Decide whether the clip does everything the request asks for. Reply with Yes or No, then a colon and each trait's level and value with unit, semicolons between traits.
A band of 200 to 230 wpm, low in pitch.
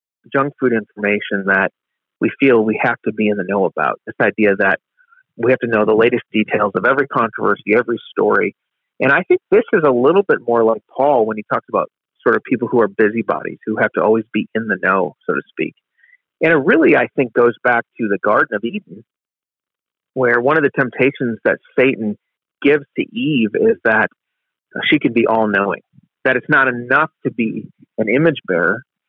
Yes: fast, 205 wpm; low, 125 Hz